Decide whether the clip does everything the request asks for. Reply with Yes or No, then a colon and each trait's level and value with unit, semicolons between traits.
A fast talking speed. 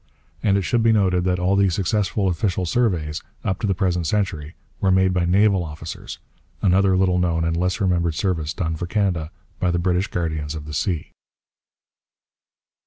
No: average, 175 wpm